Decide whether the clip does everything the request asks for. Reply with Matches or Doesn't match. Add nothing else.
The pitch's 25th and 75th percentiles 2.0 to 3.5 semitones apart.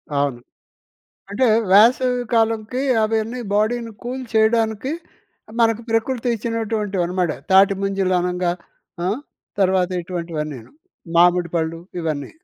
Doesn't match